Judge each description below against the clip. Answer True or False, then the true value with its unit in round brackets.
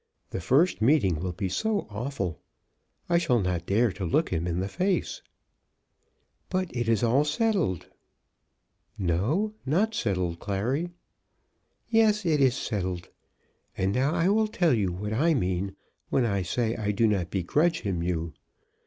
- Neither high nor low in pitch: False (115 Hz)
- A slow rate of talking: False (155 wpm)